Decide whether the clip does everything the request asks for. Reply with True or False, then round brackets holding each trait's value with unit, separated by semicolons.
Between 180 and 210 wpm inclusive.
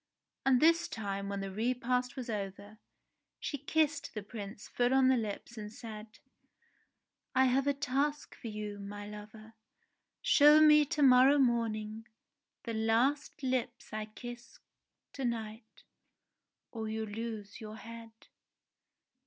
False (135 wpm)